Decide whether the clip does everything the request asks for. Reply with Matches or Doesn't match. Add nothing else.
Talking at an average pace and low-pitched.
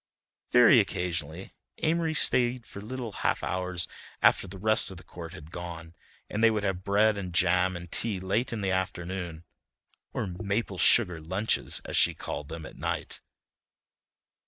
Matches